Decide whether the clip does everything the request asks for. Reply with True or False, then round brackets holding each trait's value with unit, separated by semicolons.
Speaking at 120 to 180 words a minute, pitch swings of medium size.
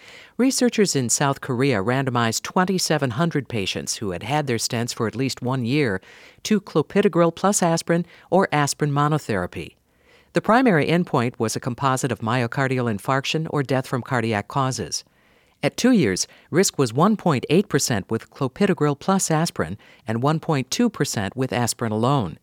False (140 wpm; 6.0 semitones)